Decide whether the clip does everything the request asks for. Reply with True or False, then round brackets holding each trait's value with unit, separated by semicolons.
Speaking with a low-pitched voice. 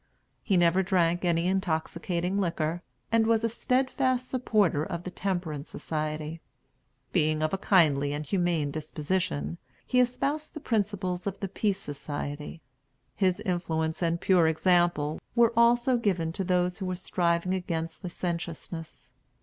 False (175 Hz)